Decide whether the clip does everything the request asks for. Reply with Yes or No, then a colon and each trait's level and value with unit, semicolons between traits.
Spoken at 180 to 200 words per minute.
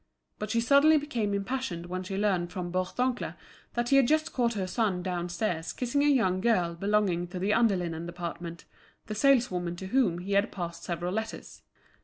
Yes: average, 185 wpm